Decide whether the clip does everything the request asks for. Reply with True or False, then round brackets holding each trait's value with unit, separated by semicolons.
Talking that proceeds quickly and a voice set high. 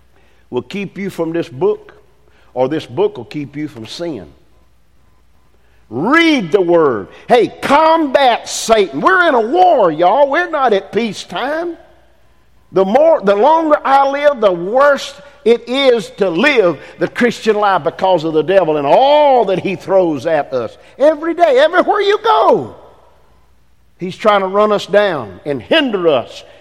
False (160 wpm; 230 Hz)